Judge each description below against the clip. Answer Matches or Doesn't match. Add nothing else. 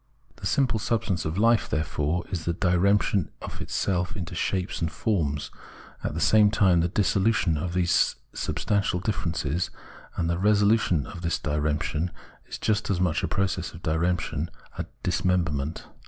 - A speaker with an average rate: Matches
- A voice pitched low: Matches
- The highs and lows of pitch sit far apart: Doesn't match